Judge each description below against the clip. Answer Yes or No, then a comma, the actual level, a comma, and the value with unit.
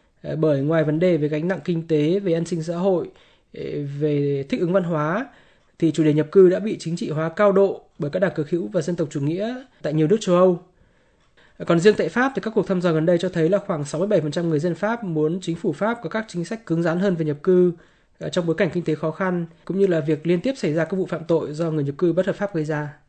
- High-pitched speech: No, medium, 175 Hz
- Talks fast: Yes, fast, 280 wpm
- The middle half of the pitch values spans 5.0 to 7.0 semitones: No, average, 3.3 semitones